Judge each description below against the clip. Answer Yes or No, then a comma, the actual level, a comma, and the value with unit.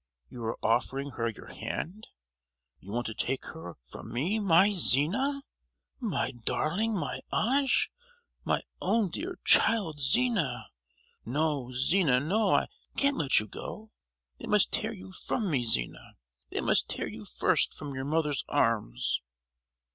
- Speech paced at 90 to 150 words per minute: Yes, average, 145 wpm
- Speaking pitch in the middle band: Yes, medium, 155 Hz